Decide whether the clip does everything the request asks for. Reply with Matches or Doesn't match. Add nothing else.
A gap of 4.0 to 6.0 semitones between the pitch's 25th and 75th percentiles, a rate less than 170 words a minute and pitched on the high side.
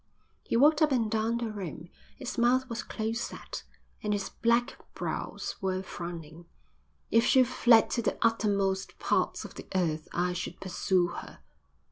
Matches